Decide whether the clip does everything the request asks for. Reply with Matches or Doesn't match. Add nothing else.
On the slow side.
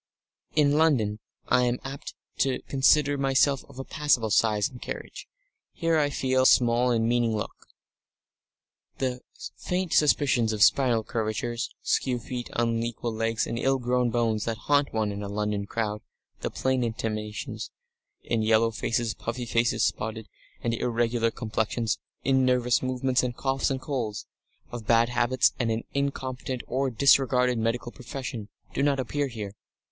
Doesn't match